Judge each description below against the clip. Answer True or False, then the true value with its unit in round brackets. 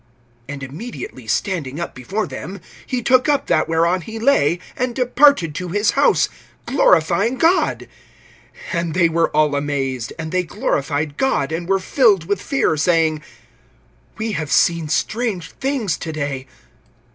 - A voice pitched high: False (170 Hz)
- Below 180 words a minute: True (145 wpm)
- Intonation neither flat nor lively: False (6.8 semitones)